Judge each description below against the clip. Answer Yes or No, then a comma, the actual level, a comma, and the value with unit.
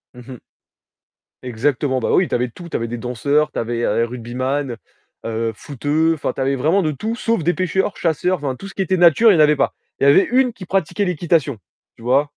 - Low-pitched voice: No, medium, 145 Hz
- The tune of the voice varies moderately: No, wide, 6.1 semitones